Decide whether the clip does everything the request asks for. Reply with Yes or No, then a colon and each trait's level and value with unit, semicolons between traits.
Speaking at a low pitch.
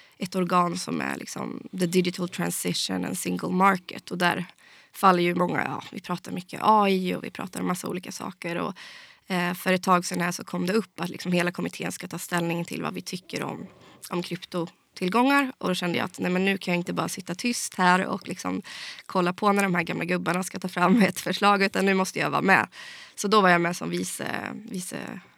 No: medium, 185 Hz